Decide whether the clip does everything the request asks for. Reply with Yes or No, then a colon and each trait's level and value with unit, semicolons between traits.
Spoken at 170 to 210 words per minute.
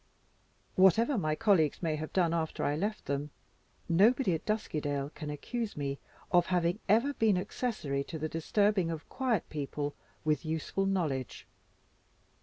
No: average, 145 wpm